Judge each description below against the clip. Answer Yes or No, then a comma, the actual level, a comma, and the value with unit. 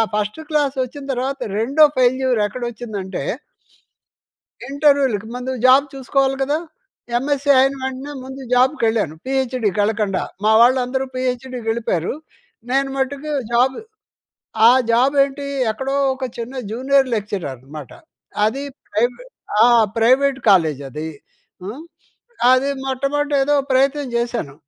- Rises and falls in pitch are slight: No, average, 3.6 semitones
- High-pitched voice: Yes, very high, 255 Hz